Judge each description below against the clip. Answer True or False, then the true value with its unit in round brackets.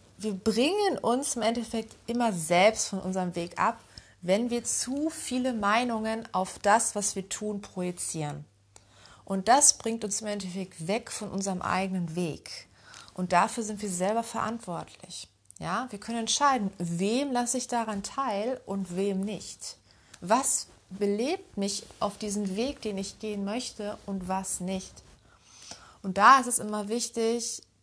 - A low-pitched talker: False (210 Hz)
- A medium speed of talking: True (150 wpm)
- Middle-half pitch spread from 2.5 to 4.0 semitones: True (3.5 semitones)